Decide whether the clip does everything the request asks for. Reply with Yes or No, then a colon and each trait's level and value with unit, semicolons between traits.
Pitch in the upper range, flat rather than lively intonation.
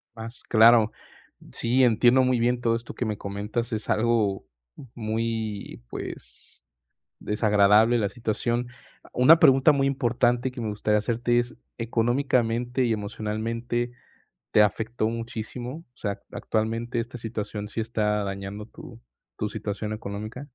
No: low, 115 Hz; narrow, 2.2 semitones